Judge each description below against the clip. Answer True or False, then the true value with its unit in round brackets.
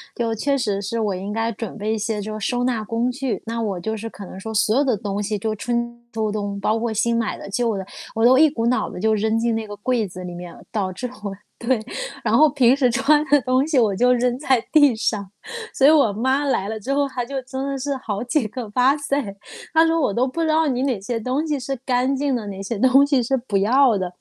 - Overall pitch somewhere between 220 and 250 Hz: True (235 Hz)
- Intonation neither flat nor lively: True (3.8 semitones)